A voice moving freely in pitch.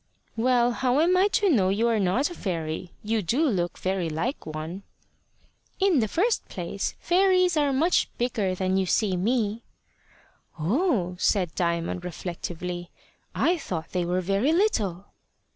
Yes: wide, 7.9 semitones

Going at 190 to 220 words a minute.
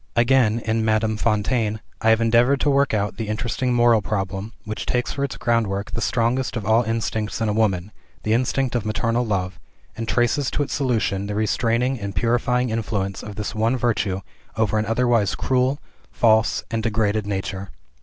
No: average, 180 wpm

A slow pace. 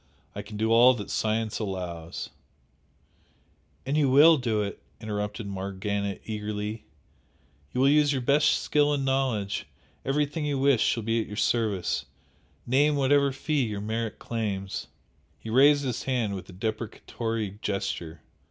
No: average, 150 wpm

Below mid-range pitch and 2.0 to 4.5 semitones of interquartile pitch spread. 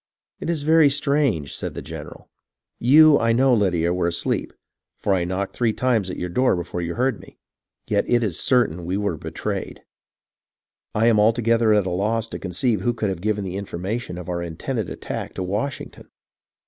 No: low, 105 Hz; average, 5.1 semitones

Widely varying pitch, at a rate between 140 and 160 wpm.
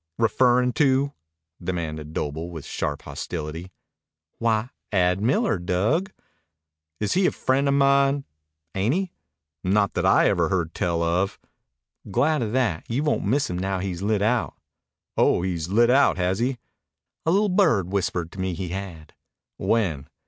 Yes: wide, 6.8 semitones; average, 155 wpm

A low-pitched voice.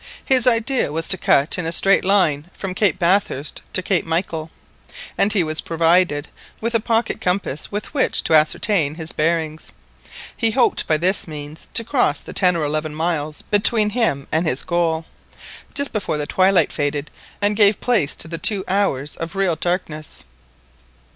No: medium, 175 Hz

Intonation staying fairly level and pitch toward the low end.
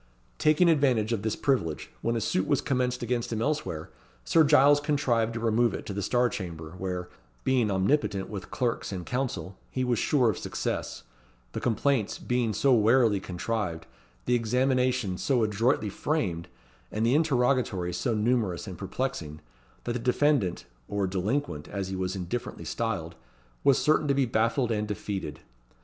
No: average, 5.0 semitones; low, 115 Hz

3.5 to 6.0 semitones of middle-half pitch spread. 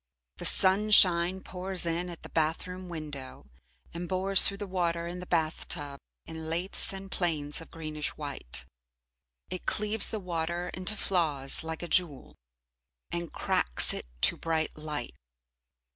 No: average, 2.8 semitones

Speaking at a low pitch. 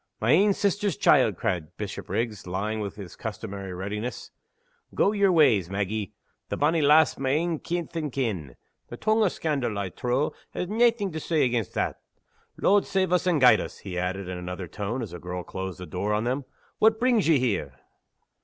Yes: low, 120 Hz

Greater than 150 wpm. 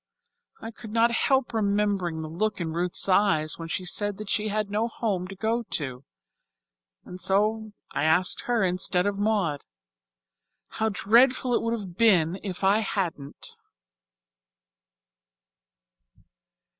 No: slow, 135 wpm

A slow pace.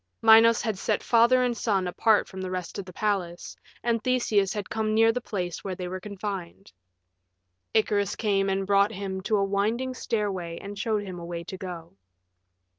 No: average, 190 wpm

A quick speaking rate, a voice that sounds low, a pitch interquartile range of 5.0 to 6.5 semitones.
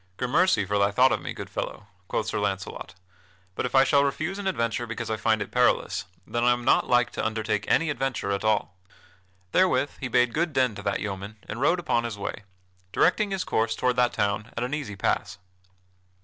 No: fast, 210 wpm; low, 120 Hz; average, 4.3 semitones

